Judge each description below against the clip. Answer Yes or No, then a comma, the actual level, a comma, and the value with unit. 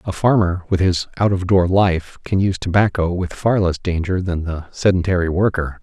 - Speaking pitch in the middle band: No, very low, 90 Hz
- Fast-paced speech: No, average, 195 wpm